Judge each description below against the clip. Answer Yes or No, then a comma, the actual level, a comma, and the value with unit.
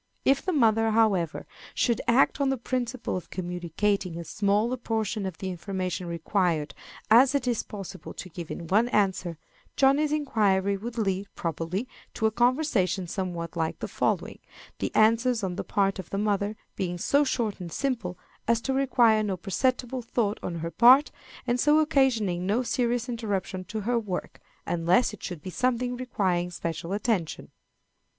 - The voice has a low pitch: No, high, 210 Hz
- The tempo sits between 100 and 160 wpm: No, average, 170 wpm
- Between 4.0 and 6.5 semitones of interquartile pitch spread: Yes, average, 5.0 semitones